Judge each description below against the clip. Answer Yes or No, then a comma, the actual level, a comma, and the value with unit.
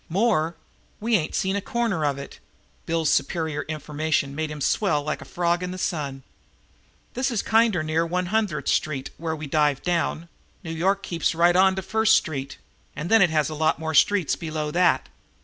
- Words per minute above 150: Yes, average, 190 wpm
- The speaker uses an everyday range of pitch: Yes, average, 3.7 semitones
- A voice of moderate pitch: Yes, medium, 165 Hz